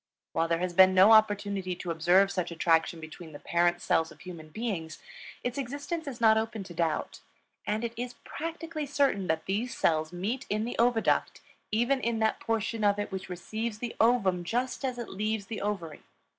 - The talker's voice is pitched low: No, high, 205 Hz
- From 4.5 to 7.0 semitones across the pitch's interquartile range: Yes, average, 5.1 semitones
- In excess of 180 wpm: Yes, average, 190 wpm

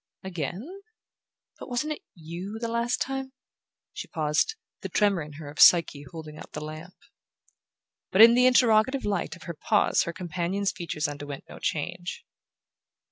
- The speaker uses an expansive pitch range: Yes, wide, 6.8 semitones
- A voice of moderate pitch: Yes, medium, 180 Hz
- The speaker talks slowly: No, average, 160 wpm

